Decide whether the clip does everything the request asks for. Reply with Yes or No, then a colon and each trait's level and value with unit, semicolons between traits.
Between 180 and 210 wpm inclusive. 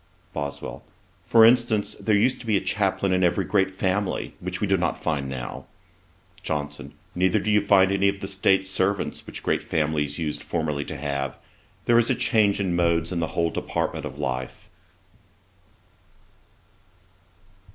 No: average, 160 wpm